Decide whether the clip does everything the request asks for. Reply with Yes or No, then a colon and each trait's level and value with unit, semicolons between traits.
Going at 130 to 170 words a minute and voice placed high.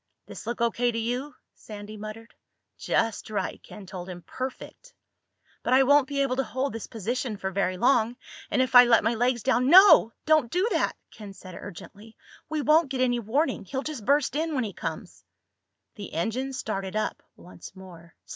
No: average, 185 wpm; high, 235 Hz